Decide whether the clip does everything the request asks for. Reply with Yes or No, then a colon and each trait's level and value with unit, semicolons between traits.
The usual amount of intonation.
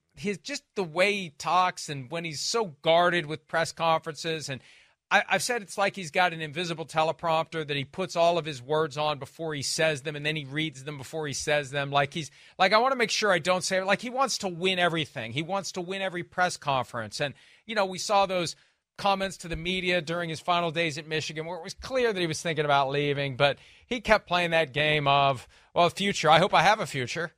Yes: average, 3.5 semitones